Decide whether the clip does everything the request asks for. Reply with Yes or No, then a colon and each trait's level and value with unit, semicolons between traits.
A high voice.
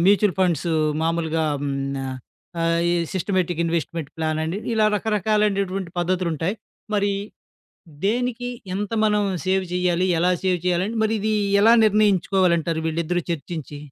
No: medium, 180 Hz